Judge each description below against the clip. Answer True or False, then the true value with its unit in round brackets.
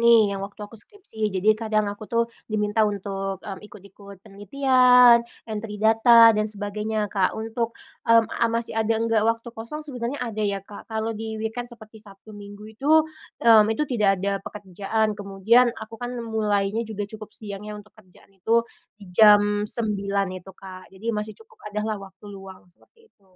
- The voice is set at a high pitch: True (215 Hz)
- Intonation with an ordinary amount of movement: False (2.2 semitones)